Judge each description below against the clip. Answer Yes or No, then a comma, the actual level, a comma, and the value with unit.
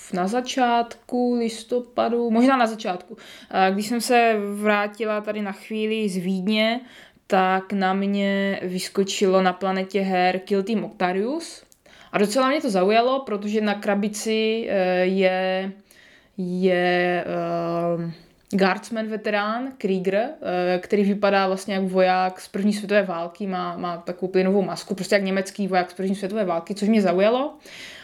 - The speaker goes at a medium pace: Yes, average, 135 wpm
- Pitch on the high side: Yes, high, 200 Hz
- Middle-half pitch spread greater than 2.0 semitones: Yes, average, 2.7 semitones